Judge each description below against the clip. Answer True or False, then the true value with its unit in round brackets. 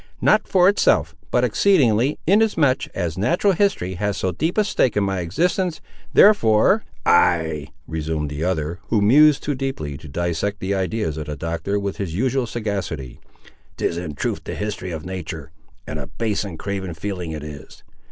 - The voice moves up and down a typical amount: False (7.9 semitones)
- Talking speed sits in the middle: True (170 wpm)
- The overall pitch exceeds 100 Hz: False (95 Hz)